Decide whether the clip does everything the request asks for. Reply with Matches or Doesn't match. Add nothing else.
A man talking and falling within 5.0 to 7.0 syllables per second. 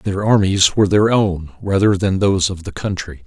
Matches